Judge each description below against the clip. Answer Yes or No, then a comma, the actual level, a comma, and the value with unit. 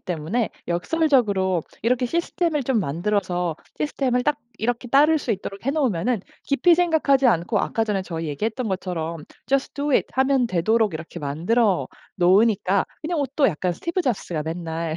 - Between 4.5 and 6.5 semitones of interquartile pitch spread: No, wide, 7.6 semitones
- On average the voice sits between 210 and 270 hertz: Yes, high, 220 Hz